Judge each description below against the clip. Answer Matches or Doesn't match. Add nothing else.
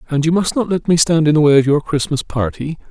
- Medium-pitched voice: Matches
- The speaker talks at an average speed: Doesn't match